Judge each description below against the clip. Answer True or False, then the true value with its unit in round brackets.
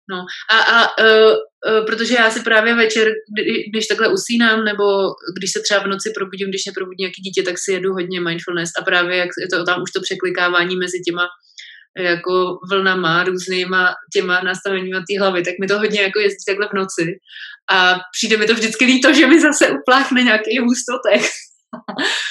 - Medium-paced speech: False (190 wpm)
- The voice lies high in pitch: True (195 Hz)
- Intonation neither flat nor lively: True (3.2 semitones)